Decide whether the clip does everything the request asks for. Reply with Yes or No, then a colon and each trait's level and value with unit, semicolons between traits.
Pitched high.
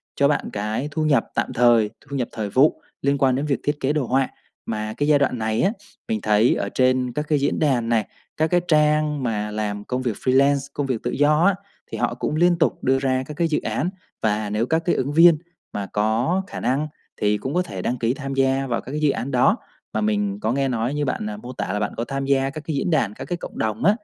No: low, 135 Hz